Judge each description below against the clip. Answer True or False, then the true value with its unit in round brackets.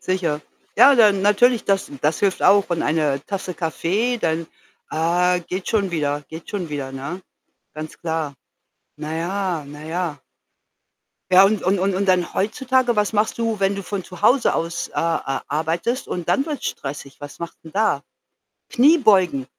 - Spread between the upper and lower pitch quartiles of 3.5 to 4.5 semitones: True (4.2 semitones)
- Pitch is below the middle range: False (180 Hz)